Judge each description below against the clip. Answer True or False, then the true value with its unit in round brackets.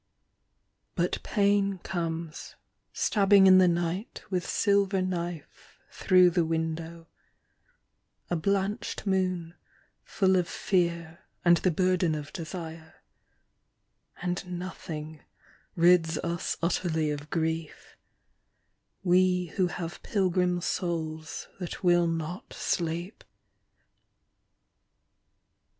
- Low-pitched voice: False (175 Hz)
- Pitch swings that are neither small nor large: False (2.1 semitones)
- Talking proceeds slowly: True (95 wpm)